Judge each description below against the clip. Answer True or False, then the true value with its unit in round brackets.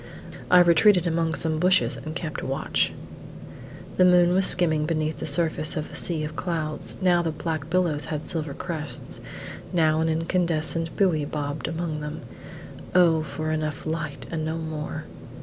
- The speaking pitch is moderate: True (160 Hz)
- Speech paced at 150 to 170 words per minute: True (160 wpm)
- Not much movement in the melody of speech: True (1.9 semitones)